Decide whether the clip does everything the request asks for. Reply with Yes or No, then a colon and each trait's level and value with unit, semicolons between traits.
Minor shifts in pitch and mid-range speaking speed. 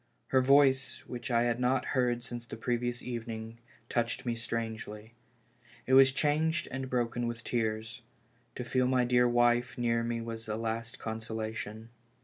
Yes: narrow, 1.6 semitones; average, 155 wpm